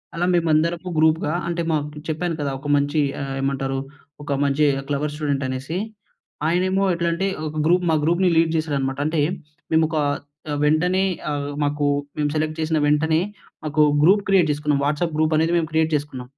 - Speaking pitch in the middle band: Yes, medium, 155 Hz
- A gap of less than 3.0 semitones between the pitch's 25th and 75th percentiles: Yes, narrow, 2.5 semitones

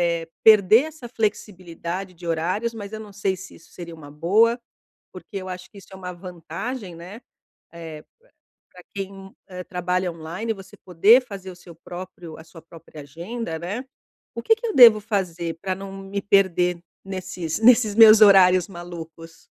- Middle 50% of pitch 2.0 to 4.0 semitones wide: Yes, average, 3.5 semitones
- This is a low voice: No, medium, 185 Hz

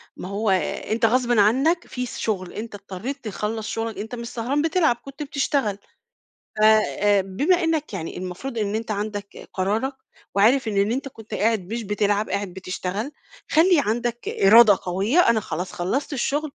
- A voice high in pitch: Yes, high, 220 Hz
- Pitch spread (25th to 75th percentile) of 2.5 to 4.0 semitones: No, average, 4.7 semitones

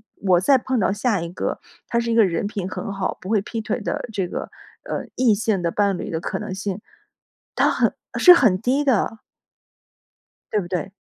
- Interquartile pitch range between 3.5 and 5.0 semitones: Yes, average, 3.8 semitones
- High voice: Yes, high, 205 Hz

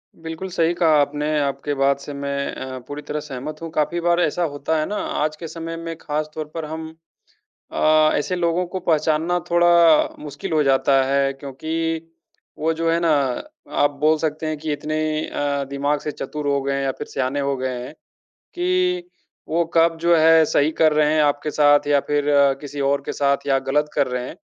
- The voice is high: No, medium, 150 Hz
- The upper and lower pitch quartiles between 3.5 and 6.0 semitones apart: No, narrow, 2.5 semitones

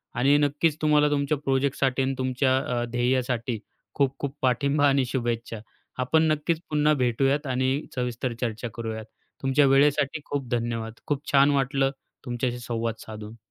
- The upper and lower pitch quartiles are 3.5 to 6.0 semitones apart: No, average, 2.7 semitones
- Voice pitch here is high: No, low, 130 Hz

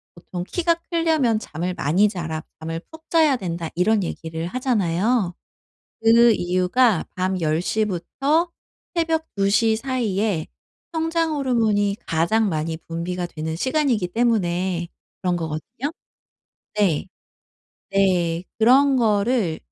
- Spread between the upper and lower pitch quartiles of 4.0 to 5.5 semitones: No, wide, 6.5 semitones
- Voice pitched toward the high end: Yes, high, 200 Hz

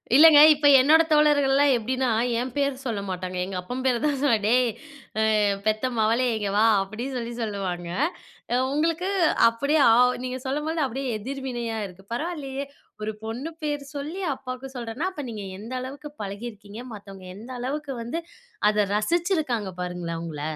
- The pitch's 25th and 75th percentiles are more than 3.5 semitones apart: Yes, average, 5.1 semitones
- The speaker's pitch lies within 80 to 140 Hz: No, very high, 250 Hz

